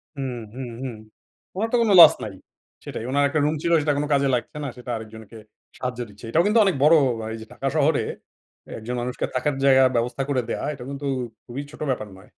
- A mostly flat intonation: No, average, 3.5 semitones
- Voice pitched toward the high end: No, low, 130 Hz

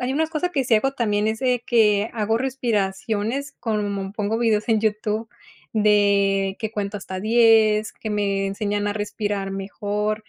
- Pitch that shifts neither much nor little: No, narrow, 1.9 semitones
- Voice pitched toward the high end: Yes, high, 215 Hz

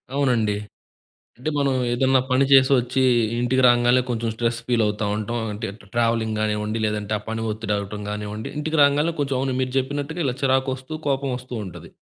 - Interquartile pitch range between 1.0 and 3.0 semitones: No, average, 3.4 semitones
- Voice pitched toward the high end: No, low, 125 Hz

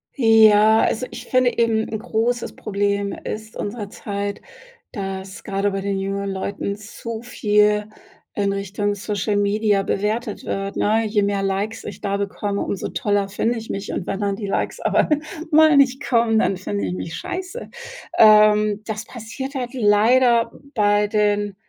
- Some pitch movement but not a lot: No, narrow, 1.9 semitones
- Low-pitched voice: No, high, 210 Hz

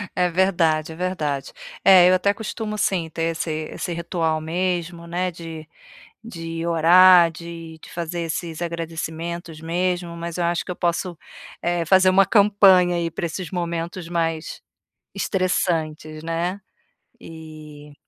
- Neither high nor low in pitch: Yes, medium, 170 Hz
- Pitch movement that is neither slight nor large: No, narrow, 1.8 semitones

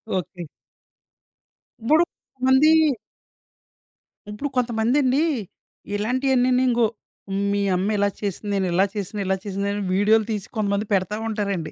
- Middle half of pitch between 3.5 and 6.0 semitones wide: Yes, average, 4.0 semitones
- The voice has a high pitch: Yes, high, 210 Hz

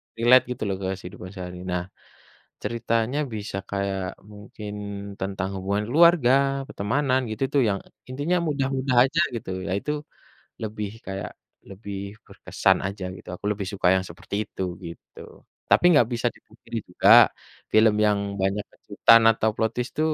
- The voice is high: No, low, 105 Hz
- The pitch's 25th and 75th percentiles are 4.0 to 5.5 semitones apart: Yes, average, 4.4 semitones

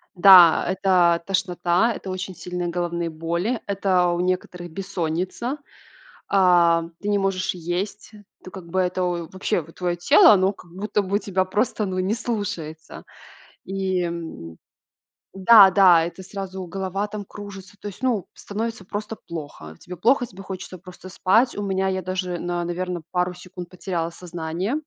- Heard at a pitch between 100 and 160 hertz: No, medium, 185 Hz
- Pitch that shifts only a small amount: Yes, narrow, 2.2 semitones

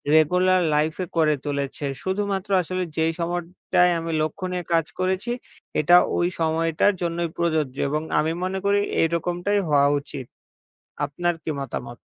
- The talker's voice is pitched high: No, medium, 170 Hz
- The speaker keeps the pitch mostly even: No, average, 3.0 semitones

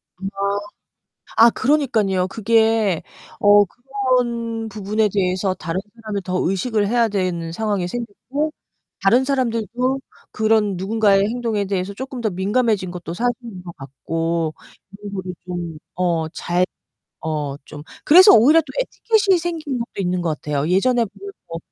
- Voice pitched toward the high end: Yes, high, 205 Hz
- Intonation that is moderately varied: Yes, average, 4.9 semitones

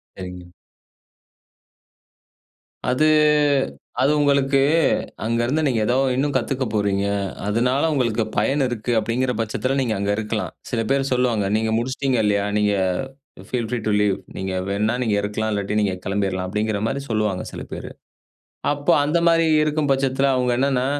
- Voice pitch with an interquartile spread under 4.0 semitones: No, average, 4.5 semitones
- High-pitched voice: No, low, 120 Hz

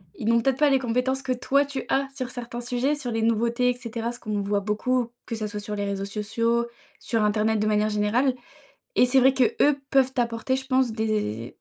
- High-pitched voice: Yes, high, 235 Hz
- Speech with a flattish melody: No, average, 3.3 semitones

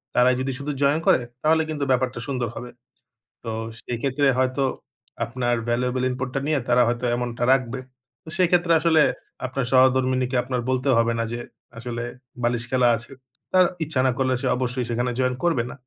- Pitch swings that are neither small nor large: No, narrow, 2.0 semitones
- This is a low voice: Yes, low, 130 Hz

